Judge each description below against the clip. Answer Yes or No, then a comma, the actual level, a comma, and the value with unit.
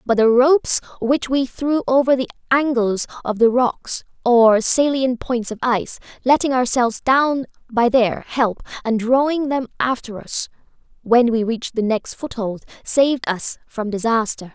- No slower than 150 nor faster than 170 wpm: Yes, average, 155 wpm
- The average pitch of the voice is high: Yes, high, 245 Hz